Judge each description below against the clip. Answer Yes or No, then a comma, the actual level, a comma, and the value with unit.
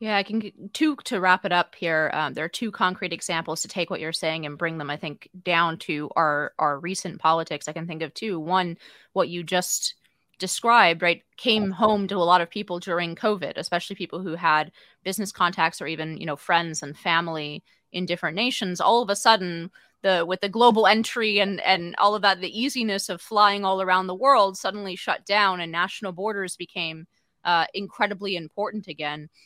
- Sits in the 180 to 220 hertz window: Yes, medium, 185 Hz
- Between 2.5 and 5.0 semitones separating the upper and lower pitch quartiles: Yes, average, 3.4 semitones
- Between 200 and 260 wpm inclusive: Yes, fast, 205 wpm